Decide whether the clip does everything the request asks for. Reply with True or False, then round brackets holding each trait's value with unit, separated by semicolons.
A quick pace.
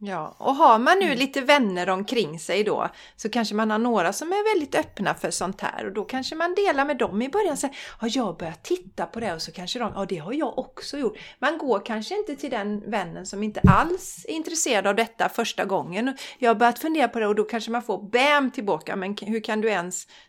True (245 wpm)